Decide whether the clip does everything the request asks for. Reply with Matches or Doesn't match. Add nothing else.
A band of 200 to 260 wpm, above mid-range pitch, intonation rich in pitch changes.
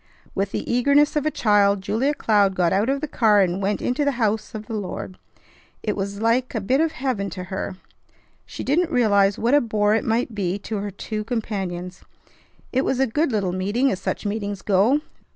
Doesn't match